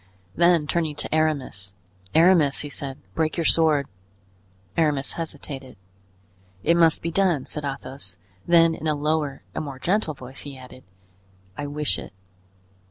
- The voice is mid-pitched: Yes, medium, 150 Hz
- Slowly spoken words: No, average, 145 wpm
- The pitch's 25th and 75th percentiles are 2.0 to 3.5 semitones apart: Yes, average, 3.0 semitones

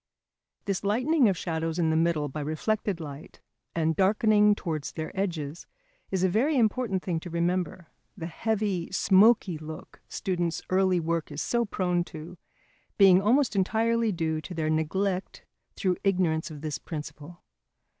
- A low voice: No, medium, 180 Hz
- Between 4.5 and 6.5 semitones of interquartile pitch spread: No, average, 4.1 semitones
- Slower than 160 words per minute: Yes, average, 150 wpm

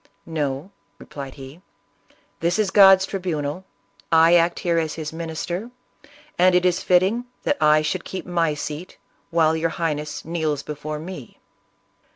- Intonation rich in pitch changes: No, average, 3.1 semitones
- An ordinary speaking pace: Yes, average, 150 wpm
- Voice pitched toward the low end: No, medium, 165 Hz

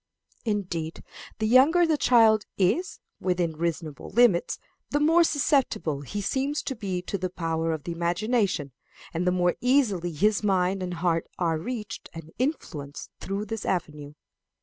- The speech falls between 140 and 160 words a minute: Yes, average, 150 wpm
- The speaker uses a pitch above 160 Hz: Yes, medium, 185 Hz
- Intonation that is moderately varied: No, wide, 5.8 semitones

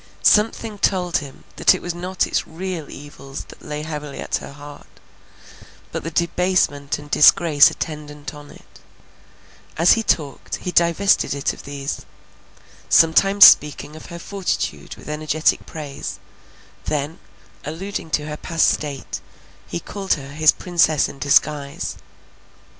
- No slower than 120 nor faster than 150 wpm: Yes, average, 140 wpm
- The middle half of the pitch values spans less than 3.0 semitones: No, average, 3.3 semitones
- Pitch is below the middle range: No, medium, 155 Hz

